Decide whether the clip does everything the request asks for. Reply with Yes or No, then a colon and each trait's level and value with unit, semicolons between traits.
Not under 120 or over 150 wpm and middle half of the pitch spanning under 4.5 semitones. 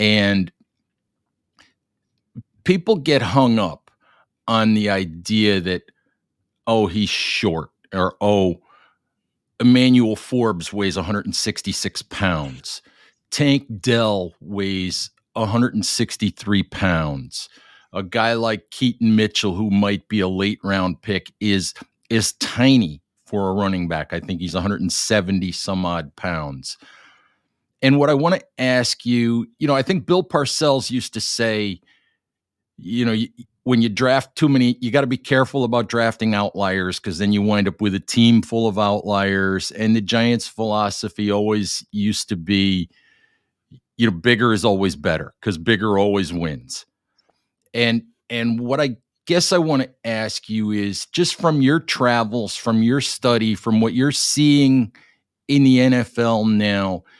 Yes: average, 145 wpm; average, 3.6 semitones